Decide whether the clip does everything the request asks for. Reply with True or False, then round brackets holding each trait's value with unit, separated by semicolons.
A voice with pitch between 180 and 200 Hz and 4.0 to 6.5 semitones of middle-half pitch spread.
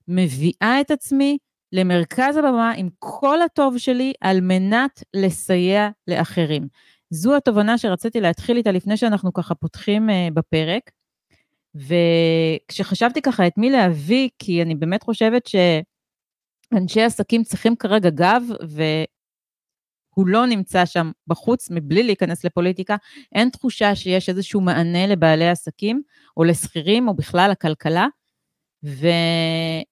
True (190 Hz; 5.4 semitones)